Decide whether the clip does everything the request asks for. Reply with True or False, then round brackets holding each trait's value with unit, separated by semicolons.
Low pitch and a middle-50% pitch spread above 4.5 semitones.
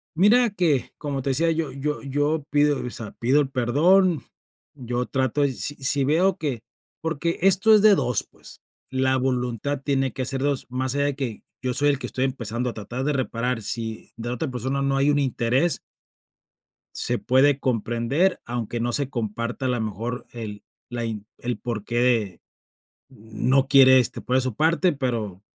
False (130 Hz; 3.4 semitones)